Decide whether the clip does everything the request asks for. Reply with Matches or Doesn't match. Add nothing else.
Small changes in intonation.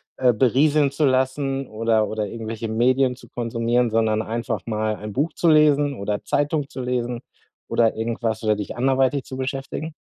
Doesn't match